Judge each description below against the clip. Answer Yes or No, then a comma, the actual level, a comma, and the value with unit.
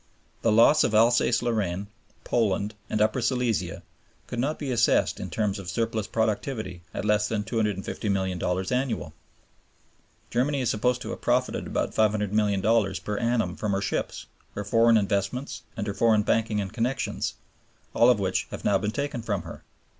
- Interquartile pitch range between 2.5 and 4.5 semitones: Yes, average, 2.8 semitones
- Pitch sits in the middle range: No, low, 110 Hz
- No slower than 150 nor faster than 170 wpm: Yes, average, 160 wpm